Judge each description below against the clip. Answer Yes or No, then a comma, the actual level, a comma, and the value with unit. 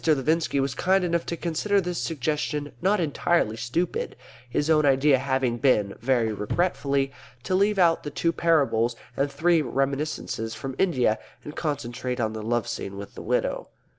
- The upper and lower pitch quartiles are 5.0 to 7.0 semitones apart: Yes, wide, 5.6 semitones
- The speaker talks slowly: No, average, 165 wpm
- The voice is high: No, medium, 140 Hz